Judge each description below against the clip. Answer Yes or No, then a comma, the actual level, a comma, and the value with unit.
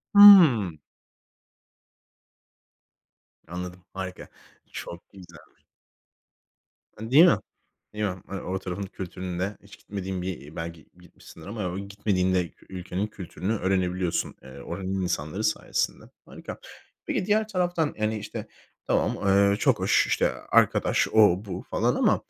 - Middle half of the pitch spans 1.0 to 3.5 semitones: Yes, average, 2.9 semitones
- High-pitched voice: No, very low, 95 Hz